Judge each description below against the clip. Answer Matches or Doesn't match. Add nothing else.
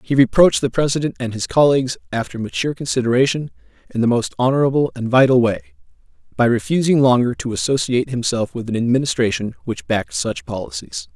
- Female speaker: Doesn't match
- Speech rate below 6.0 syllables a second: Doesn't match